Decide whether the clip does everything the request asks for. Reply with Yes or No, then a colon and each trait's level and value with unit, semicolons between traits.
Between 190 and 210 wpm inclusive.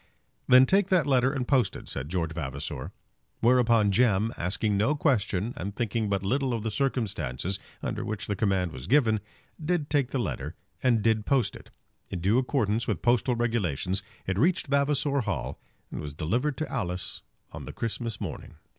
No: average, 175 wpm